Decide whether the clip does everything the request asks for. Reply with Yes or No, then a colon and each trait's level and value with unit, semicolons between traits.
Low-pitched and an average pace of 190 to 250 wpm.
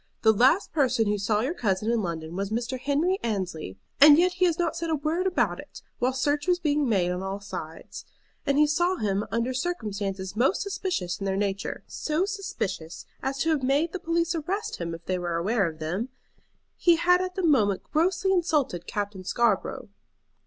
No: very high, 255 Hz; average, 195 wpm